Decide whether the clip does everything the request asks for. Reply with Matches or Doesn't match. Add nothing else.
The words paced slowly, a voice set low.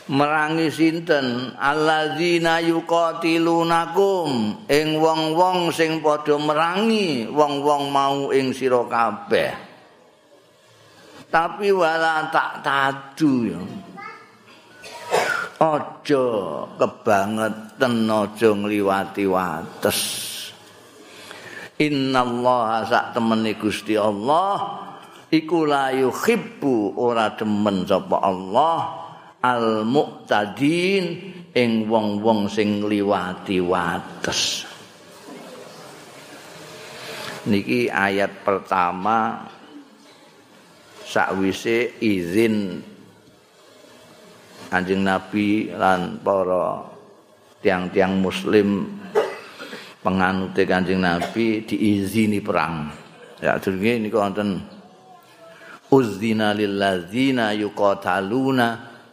Matches